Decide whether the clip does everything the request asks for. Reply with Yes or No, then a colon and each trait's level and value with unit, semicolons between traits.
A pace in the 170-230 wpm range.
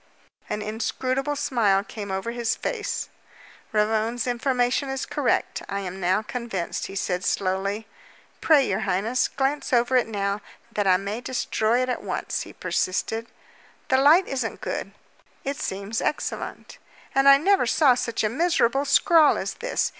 No: average, 155 wpm